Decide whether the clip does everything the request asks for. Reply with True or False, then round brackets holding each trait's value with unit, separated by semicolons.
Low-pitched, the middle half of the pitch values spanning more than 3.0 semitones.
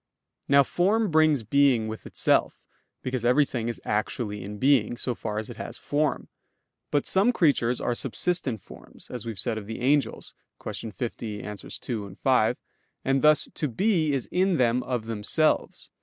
True (125 Hz; 5.1 semitones)